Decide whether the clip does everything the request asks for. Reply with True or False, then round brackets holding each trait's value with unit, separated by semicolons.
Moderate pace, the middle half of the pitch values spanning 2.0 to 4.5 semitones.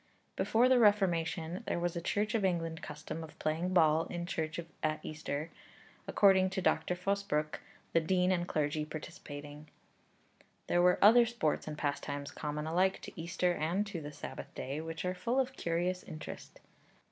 True (165 wpm; 3.4 semitones)